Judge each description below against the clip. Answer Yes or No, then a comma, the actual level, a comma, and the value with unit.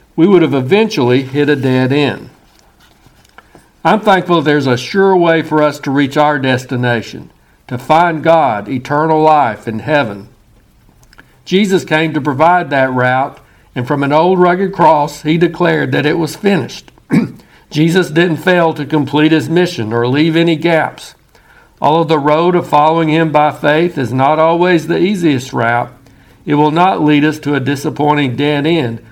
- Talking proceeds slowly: No, average, 165 wpm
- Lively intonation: No, average, 3.7 semitones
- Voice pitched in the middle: Yes, medium, 150 Hz